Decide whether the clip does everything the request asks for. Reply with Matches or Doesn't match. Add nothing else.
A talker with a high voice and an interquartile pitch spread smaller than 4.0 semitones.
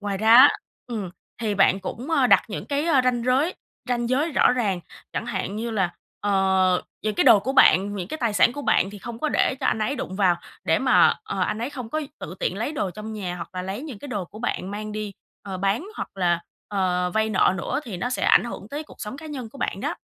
Doesn't match